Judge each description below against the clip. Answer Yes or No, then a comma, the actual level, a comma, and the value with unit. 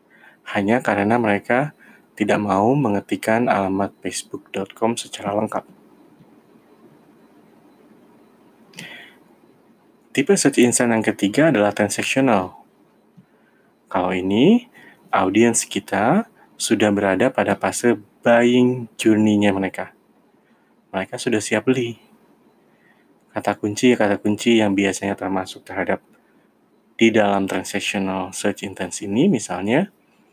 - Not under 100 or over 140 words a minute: No, average, 90 wpm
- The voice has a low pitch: Yes, low, 105 Hz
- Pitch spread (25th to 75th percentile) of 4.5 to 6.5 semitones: No, average, 3.2 semitones